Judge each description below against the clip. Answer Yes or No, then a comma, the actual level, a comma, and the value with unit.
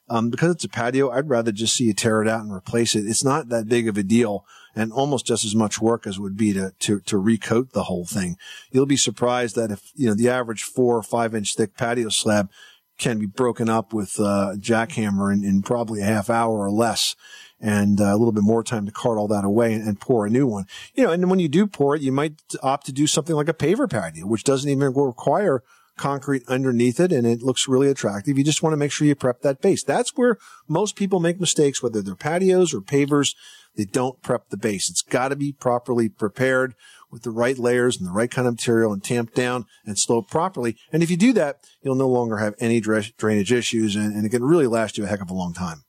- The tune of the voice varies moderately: Yes, average, 4.1 semitones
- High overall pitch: No, low, 120 Hz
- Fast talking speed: Yes, fast, 245 wpm